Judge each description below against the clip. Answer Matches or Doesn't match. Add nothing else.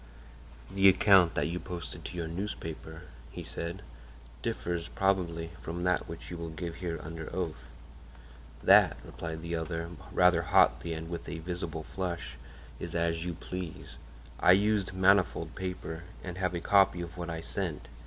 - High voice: Doesn't match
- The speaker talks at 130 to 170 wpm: Matches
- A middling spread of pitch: Doesn't match